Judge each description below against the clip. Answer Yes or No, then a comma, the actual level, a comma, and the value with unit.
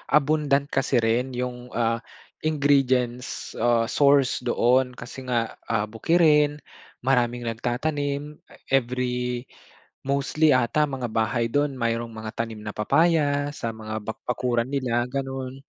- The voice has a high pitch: No, low, 125 Hz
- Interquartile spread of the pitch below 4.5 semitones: Yes, average, 3.2 semitones